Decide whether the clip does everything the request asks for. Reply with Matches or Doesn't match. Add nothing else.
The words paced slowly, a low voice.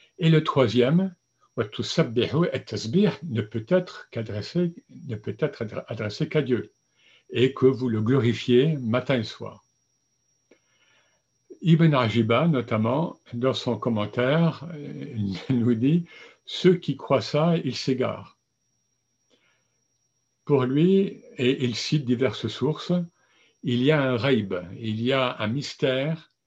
Matches